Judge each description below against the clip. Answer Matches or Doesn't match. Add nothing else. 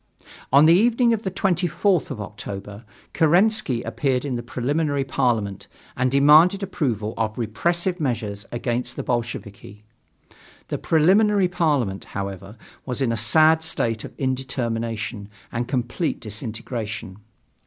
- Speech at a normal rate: Doesn't match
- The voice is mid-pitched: Doesn't match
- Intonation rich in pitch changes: Matches